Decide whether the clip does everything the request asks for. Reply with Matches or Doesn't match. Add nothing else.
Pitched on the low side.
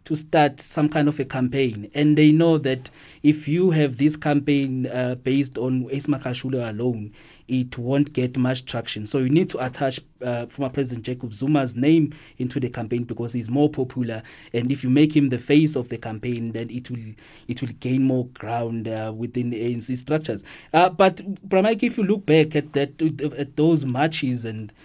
Matches